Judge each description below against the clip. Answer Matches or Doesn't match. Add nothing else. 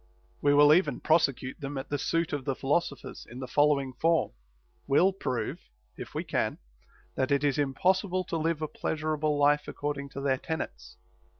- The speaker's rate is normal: Matches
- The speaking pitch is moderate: Matches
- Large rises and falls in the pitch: Doesn't match